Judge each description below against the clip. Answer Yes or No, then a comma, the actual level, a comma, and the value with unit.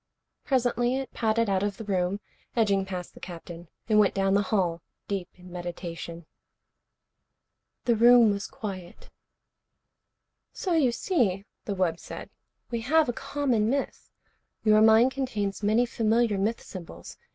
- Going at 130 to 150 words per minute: Yes, average, 140 wpm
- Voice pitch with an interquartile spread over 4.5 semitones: No, average, 4.2 semitones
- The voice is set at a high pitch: Yes, high, 210 Hz